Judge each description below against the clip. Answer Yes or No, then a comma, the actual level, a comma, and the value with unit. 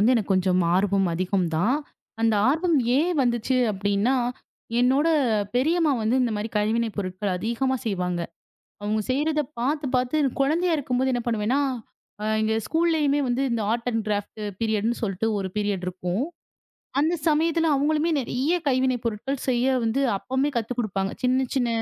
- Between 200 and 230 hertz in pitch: No, high, 245 Hz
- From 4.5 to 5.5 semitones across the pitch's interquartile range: Yes, average, 4.8 semitones